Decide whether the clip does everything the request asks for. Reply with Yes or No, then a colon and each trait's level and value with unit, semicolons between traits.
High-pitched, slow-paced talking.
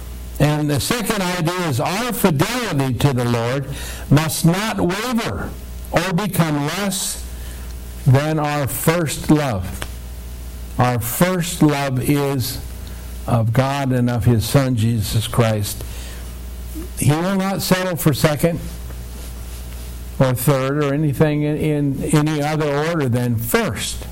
No: low, 135 Hz; slow, 120 wpm